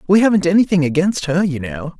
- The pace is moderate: No, fast, 210 wpm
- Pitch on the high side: No, medium, 170 Hz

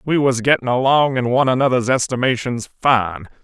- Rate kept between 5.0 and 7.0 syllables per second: Yes, 5.5 syllables/s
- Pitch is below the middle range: Yes, low, 125 Hz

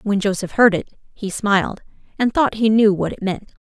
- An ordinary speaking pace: No, fast, 215 wpm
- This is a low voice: No, high, 205 Hz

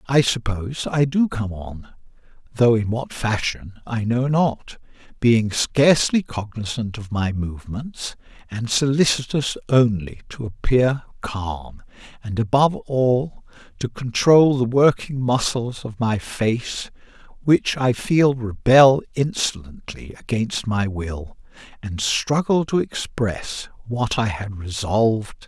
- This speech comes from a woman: No, male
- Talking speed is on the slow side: Yes, slow, 125 wpm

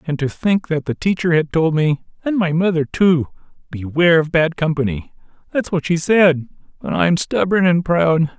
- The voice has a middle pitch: Yes, medium, 165 Hz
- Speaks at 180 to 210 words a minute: No, average, 170 wpm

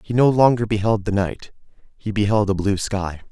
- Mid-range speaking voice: No, low, 105 Hz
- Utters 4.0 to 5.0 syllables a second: No, 5.2 syllables/s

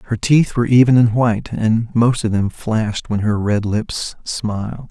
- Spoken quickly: No, average, 195 wpm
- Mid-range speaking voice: No, low, 115 Hz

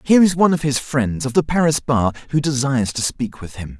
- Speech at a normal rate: No, fast, 255 wpm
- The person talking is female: No, male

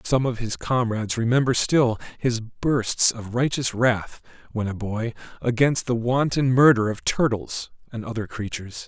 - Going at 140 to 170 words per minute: Yes, average, 155 wpm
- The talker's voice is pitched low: Yes, low, 120 Hz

